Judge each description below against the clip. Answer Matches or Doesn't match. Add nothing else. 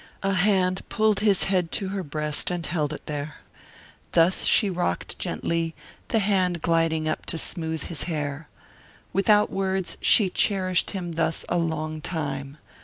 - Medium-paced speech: Matches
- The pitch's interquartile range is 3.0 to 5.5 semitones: Matches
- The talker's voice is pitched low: Doesn't match